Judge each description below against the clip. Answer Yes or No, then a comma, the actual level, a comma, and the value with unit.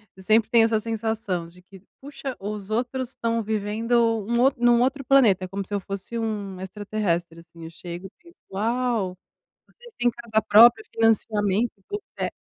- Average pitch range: Yes, average, 3.5 semitones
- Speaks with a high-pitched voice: Yes, high, 220 Hz